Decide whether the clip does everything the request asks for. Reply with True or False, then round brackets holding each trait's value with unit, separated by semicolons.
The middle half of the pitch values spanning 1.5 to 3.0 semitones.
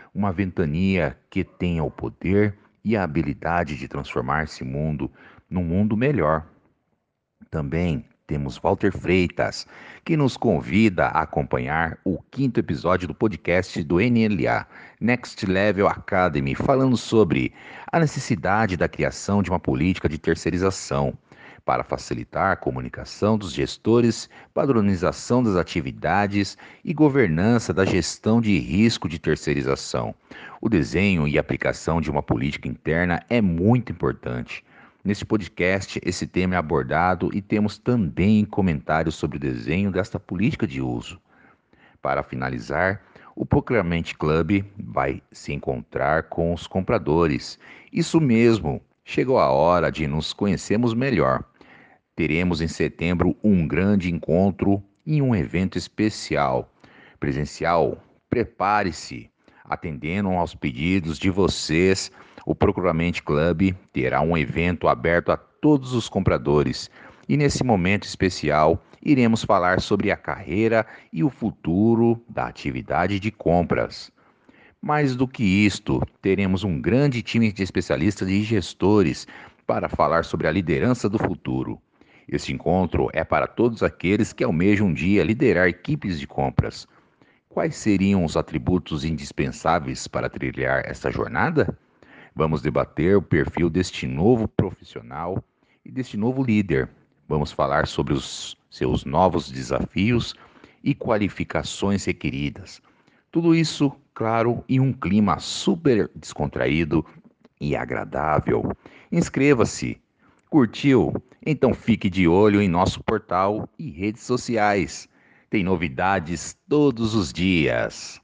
False (5.3 semitones)